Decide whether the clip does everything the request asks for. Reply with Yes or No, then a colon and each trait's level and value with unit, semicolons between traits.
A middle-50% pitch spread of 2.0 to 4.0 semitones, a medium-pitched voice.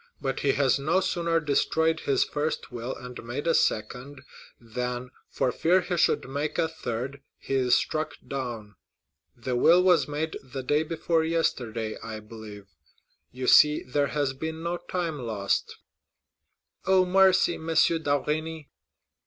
No: average, 4.6 semitones; medium, 145 Hz